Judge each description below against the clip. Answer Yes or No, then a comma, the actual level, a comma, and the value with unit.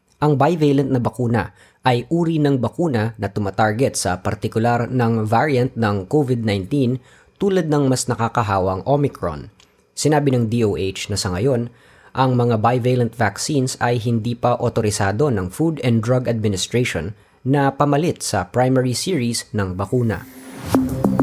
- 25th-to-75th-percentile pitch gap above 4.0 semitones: No, average, 3.4 semitones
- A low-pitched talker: Yes, low, 120 Hz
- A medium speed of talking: Yes, average, 135 wpm